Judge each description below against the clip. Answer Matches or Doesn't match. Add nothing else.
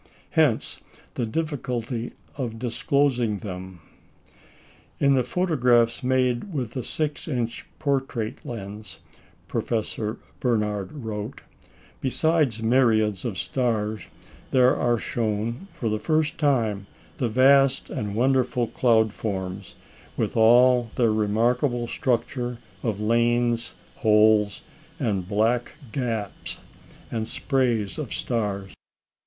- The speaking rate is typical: Doesn't match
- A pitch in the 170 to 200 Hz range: Doesn't match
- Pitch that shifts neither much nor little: Matches